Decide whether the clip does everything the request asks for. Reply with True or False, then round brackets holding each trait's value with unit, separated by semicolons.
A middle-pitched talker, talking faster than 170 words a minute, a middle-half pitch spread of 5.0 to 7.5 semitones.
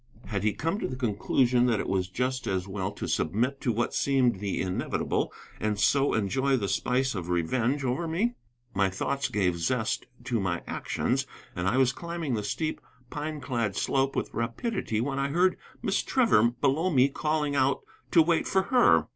False (125 Hz; 185 wpm; 5.5 semitones)